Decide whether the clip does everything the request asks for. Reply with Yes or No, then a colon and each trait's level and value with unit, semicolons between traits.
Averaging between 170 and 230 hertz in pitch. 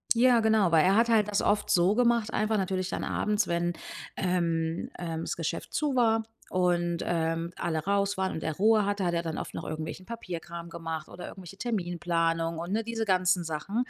Yes: medium, 185 Hz